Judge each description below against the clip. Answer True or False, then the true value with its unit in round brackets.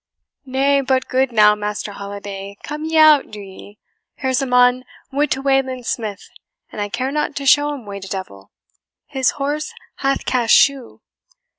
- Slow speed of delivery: False (170 wpm)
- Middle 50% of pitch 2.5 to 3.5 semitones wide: False (5.0 semitones)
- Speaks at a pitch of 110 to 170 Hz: False (255 Hz)